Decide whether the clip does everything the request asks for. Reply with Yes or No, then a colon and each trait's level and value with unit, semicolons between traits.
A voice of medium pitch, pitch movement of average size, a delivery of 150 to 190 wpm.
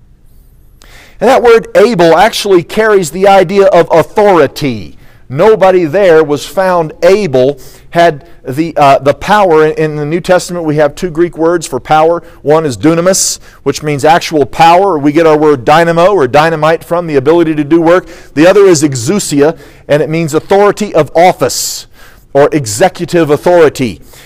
Yes: medium, 165 Hz; average, 3.2 semitones; average, 160 wpm